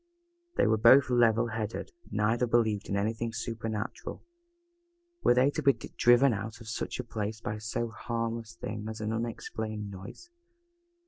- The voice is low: Yes, low, 115 Hz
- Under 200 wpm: Yes, average, 165 wpm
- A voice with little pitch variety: Yes, narrow, 1.5 semitones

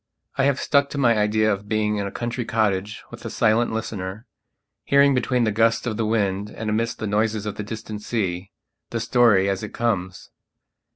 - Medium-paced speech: Yes, average, 195 wpm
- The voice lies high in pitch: No, low, 110 Hz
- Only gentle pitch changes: Yes, narrow, 2.3 semitones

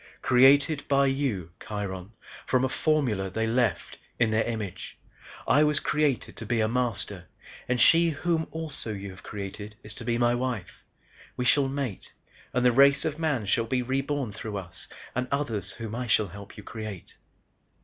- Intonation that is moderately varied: Yes, average, 4.8 semitones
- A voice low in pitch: Yes, low, 120 Hz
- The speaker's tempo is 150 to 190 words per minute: Yes, average, 175 wpm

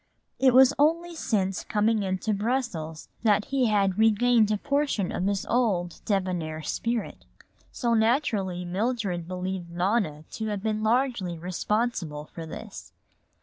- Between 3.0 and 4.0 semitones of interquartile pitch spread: No, average, 4.5 semitones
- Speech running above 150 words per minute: No, slow, 135 wpm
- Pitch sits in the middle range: No, high, 210 Hz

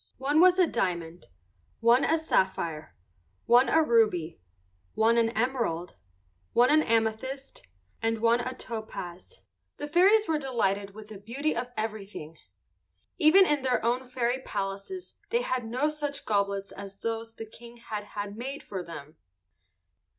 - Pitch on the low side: No, high, 230 Hz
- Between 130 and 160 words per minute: Yes, average, 145 wpm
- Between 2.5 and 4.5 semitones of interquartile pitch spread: No, average, 5.1 semitones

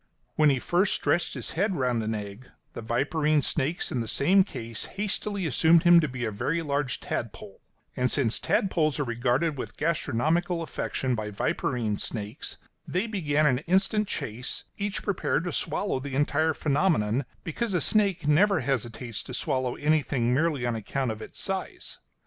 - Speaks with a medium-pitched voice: Yes, medium, 145 Hz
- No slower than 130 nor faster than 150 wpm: No, average, 165 wpm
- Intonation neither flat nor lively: No, wide, 5.9 semitones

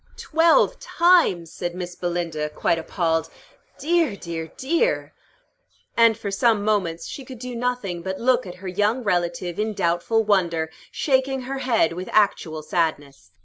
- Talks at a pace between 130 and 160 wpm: Yes, average, 145 wpm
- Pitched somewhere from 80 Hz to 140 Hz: No, high, 195 Hz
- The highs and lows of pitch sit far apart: Yes, wide, 6.5 semitones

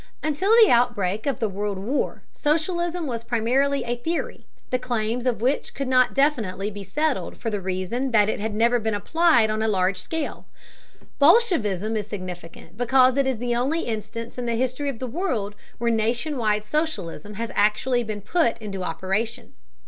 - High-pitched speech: Yes, high, 235 Hz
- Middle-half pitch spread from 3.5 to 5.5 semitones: Yes, average, 4.4 semitones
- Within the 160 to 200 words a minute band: Yes, average, 180 wpm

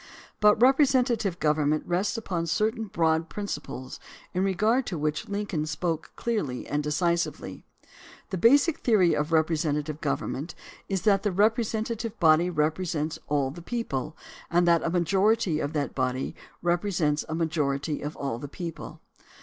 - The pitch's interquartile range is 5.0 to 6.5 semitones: Yes, wide, 5.4 semitones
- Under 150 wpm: Yes, average, 140 wpm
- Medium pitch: Yes, medium, 170 Hz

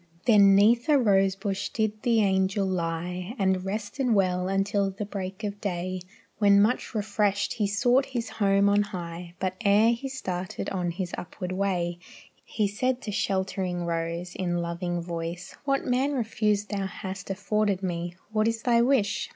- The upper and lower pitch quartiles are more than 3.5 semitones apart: No, average, 2.9 semitones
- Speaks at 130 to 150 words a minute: No, average, 165 wpm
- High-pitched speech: Yes, high, 195 Hz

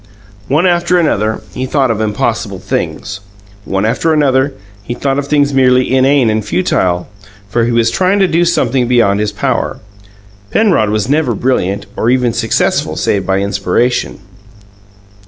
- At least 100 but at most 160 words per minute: Yes, average, 155 wpm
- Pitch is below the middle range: Yes, low, 120 Hz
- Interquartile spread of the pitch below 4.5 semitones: No, average, 5.2 semitones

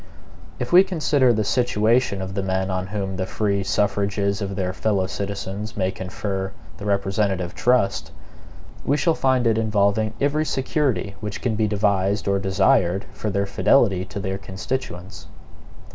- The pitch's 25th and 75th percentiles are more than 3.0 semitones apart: No, narrow, 2.5 semitones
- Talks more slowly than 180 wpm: Yes, average, 155 wpm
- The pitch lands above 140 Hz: No, low, 100 Hz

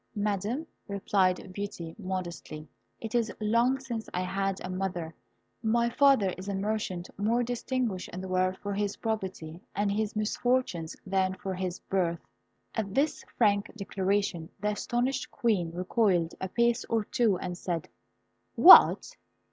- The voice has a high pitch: Yes, high, 200 Hz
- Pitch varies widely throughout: No, average, 3.4 semitones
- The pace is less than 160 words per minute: Yes, average, 145 wpm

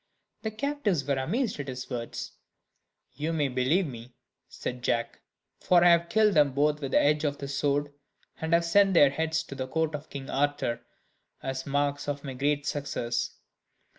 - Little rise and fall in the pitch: No, average, 3.2 semitones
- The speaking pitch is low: No, medium, 145 Hz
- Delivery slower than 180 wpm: No, average, 185 wpm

